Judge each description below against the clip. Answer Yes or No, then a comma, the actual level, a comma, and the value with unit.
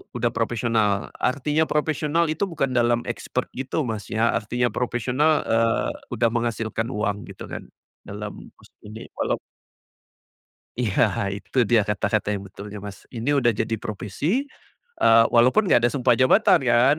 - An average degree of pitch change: Yes, average, 3.6 semitones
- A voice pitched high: No, low, 120 Hz